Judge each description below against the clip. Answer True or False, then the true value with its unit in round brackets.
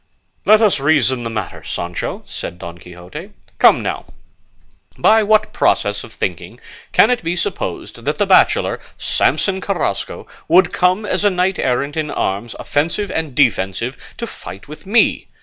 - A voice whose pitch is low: False (155 Hz)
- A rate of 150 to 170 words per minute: True (155 wpm)